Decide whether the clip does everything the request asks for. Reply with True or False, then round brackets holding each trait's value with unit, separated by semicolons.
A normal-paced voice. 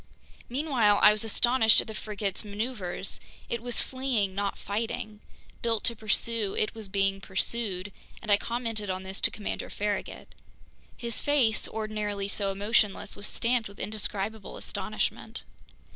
True (145 wpm)